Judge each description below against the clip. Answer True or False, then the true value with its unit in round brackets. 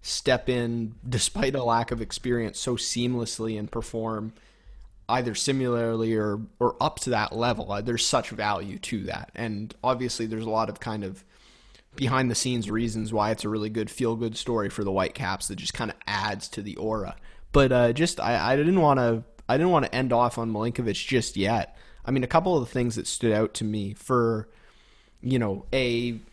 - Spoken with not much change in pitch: True (2.1 semitones)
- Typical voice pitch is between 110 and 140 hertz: True (115 Hz)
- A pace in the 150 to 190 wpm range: False (205 wpm)